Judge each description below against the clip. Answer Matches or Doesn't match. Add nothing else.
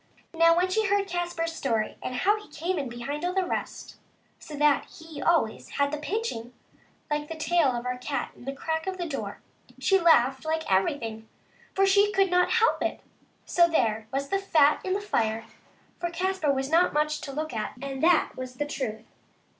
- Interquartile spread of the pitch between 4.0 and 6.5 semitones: Matches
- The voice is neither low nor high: Doesn't match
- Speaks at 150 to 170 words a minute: Doesn't match